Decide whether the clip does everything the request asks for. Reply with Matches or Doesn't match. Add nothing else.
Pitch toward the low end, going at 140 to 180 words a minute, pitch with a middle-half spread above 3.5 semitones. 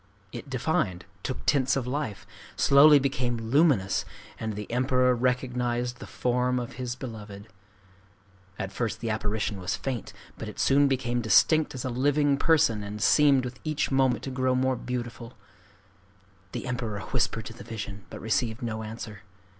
Doesn't match